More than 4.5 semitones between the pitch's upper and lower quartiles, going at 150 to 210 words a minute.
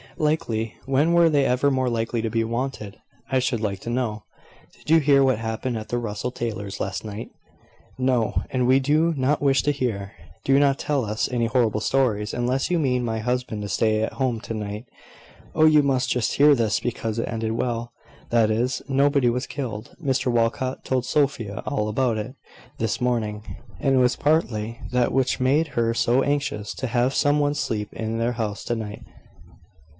No: average, 3.3 semitones; average, 190 wpm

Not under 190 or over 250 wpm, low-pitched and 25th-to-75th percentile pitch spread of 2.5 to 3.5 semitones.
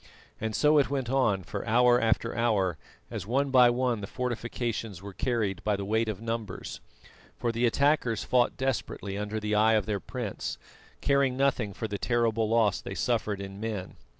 No: average, 180 wpm; low, 115 Hz; average, 3.1 semitones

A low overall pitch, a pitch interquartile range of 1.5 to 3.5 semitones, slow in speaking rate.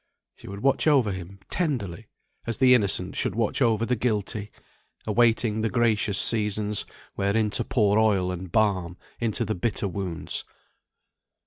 No: low, 105 Hz; average, 2.8 semitones; average, 145 wpm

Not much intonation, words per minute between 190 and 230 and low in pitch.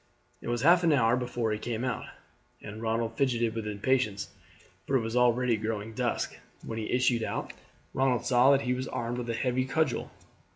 Yes: narrow, 2.2 semitones; average, 200 wpm; low, 120 Hz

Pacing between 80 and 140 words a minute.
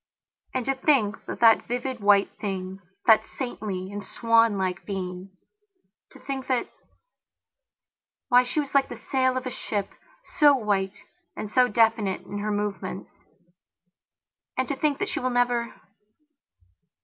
Yes: slow, 135 wpm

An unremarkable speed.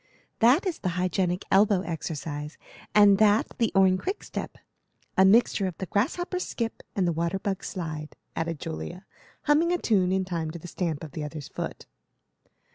Yes: average, 170 wpm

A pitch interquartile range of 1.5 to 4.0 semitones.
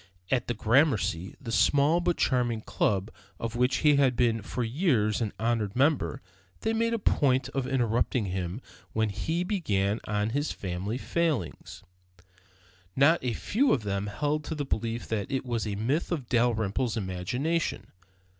No: average, 5.2 semitones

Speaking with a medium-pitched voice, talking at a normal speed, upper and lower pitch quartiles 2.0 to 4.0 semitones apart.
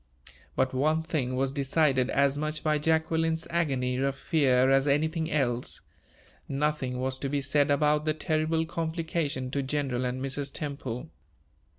Yes: medium, 145 Hz; average, 150 wpm; average, 2.9 semitones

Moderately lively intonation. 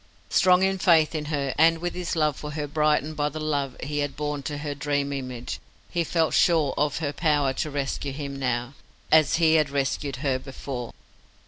No: narrow, 2.2 semitones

